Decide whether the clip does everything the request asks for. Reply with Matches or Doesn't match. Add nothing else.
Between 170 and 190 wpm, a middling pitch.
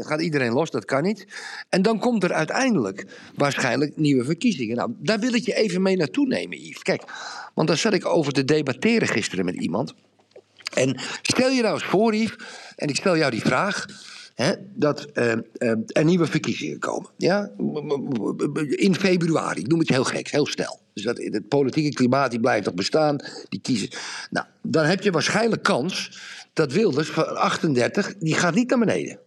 Matches